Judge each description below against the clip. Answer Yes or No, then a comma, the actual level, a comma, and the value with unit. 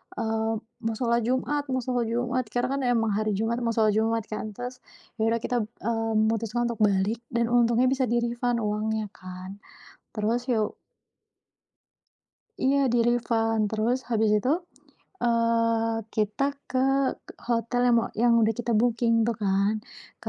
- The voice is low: No, high, 230 Hz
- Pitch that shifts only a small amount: Yes, narrow, 1.6 semitones